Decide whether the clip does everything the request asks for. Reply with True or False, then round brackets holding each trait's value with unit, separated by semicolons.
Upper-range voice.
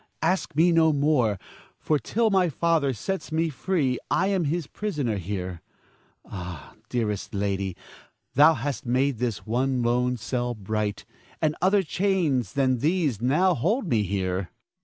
False (135 Hz)